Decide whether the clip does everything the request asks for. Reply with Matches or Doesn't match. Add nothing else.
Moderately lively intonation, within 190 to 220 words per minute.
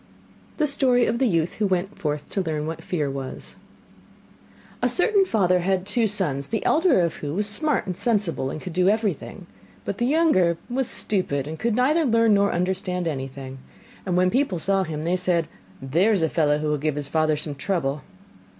Doesn't match